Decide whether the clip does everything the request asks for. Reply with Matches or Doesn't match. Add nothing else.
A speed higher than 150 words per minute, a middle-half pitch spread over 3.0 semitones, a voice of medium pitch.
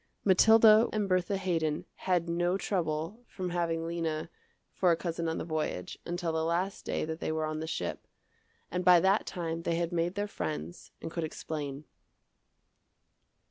Doesn't match